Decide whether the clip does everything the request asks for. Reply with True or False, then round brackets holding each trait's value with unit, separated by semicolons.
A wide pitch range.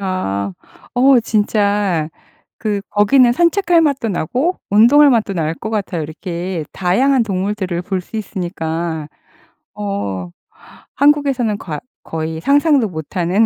True (6.9 semitones)